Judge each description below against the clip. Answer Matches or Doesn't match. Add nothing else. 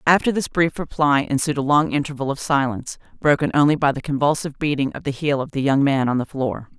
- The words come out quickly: Matches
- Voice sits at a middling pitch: Matches